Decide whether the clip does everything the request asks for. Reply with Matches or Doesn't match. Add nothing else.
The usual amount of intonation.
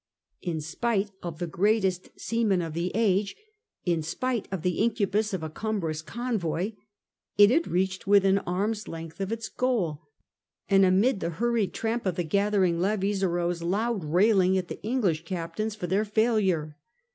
Matches